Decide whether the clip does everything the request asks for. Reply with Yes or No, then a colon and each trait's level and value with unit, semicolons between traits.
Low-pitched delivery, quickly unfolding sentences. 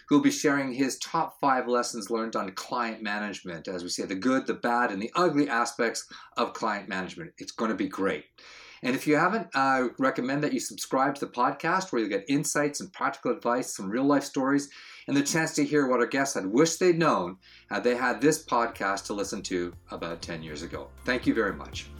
Yes: low, 130 Hz; fast, 220 wpm